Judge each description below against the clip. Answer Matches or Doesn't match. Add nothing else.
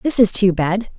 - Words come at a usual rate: Doesn't match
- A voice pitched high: Matches